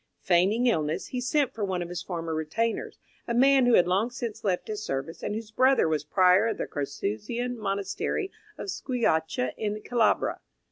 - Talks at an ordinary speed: Yes, average, 180 wpm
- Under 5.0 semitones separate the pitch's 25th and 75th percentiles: No, wide, 5.6 semitones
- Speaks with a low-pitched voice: No, high, 205 Hz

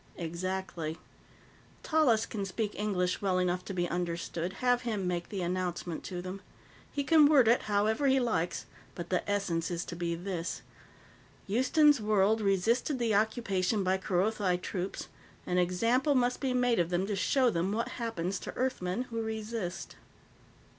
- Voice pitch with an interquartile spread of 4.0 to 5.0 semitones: Yes, average, 4.4 semitones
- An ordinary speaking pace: Yes, average, 160 wpm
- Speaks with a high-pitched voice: Yes, high, 195 Hz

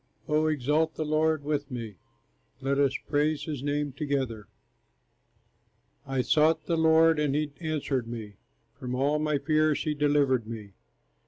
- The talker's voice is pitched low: No, medium, 145 Hz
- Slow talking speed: No, average, 145 wpm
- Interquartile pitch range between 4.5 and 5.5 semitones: No, average, 2.8 semitones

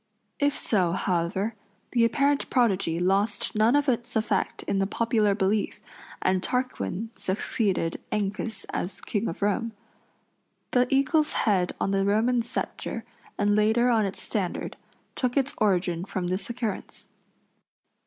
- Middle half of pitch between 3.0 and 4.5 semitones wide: Yes, average, 3.8 semitones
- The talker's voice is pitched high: Yes, high, 215 Hz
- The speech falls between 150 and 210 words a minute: No, slow, 135 wpm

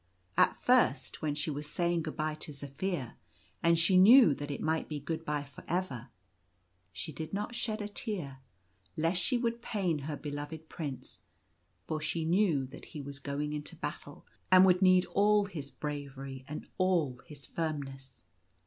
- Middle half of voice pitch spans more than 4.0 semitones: Yes, average, 4.4 semitones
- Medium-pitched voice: Yes, medium, 155 Hz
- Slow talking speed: No, average, 175 wpm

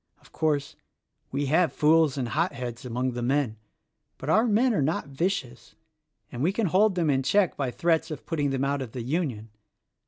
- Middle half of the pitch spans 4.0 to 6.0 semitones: Yes, average, 4.9 semitones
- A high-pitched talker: No, medium, 145 Hz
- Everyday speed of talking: Yes, average, 190 wpm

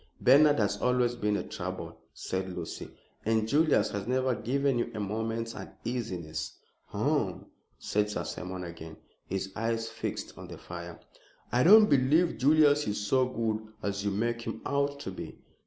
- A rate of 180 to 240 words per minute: No, average, 160 wpm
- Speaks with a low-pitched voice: Yes, low, 115 Hz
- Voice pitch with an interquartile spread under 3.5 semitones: No, average, 4.4 semitones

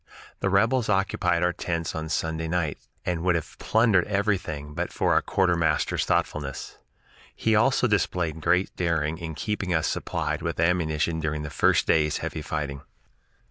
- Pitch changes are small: No, average, 3.5 semitones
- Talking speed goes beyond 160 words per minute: No, average, 155 wpm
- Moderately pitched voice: No, very low, 85 Hz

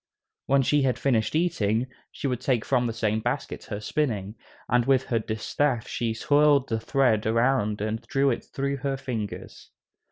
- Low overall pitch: Yes, low, 125 Hz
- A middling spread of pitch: Yes, average, 3.7 semitones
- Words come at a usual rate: Yes, average, 170 wpm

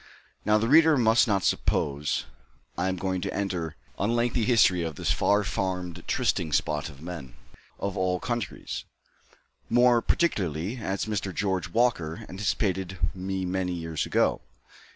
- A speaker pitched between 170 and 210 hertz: No, very low, 95 Hz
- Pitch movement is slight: No, average, 4.0 semitones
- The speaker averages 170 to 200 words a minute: No, average, 150 wpm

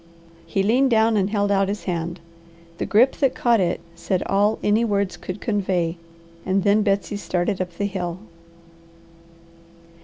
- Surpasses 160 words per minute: No, average, 155 wpm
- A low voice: No, high, 200 Hz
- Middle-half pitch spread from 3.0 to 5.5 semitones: No, narrow, 2.6 semitones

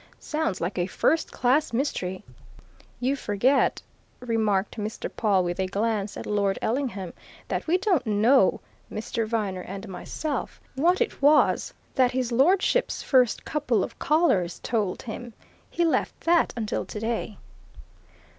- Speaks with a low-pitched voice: No, high, 230 Hz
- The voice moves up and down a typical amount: No, wide, 5.7 semitones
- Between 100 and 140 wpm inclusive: Yes, slow, 135 wpm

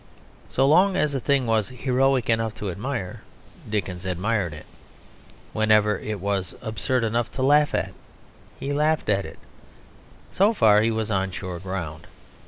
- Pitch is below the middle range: Yes, low, 110 Hz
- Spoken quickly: No, average, 155 wpm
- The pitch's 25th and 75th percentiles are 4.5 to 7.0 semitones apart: Yes, wide, 5.5 semitones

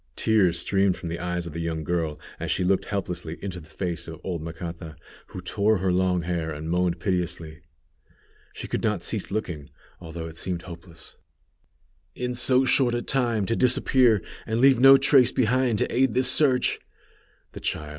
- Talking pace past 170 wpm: Yes, average, 180 wpm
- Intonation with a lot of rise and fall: Yes, wide, 6.2 semitones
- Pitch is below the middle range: Yes, very low, 90 Hz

